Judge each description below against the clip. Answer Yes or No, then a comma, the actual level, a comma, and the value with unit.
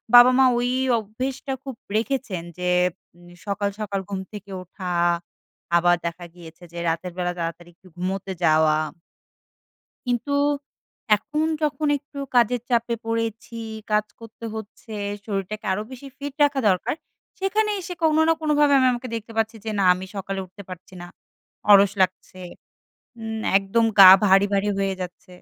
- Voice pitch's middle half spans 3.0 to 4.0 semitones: No, average, 5.0 semitones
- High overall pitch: Yes, high, 210 Hz